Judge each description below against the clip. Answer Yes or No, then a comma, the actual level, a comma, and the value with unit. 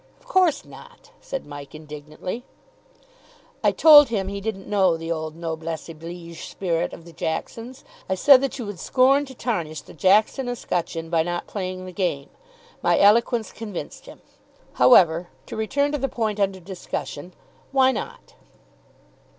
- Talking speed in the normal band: Yes, average, 155 wpm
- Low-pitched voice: No, high, 190 Hz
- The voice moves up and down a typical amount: No, wide, 6.7 semitones